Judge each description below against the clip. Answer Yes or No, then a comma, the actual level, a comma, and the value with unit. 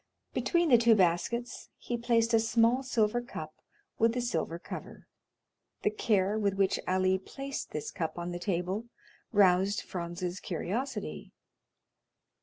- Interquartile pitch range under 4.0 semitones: No, average, 4.7 semitones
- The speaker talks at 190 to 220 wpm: No, slow, 135 wpm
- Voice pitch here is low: No, high, 205 Hz